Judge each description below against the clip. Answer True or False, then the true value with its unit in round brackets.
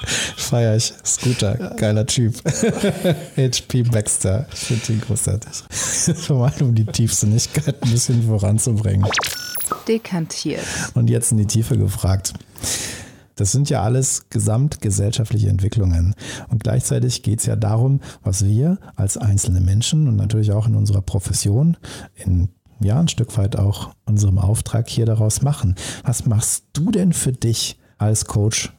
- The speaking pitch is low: True (115 Hz)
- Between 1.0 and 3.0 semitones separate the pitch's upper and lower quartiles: False (4.0 semitones)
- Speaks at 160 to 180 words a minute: False (140 wpm)